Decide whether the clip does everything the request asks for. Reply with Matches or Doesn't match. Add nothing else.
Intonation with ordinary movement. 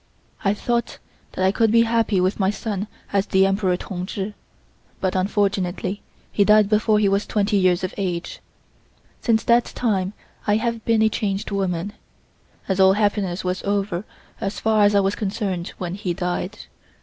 Doesn't match